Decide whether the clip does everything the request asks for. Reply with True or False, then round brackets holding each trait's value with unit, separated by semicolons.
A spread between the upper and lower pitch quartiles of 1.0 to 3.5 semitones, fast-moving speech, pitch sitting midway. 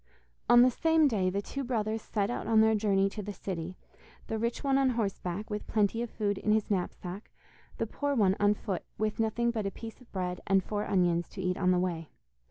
False (3.1 semitones; 225 wpm; 210 Hz)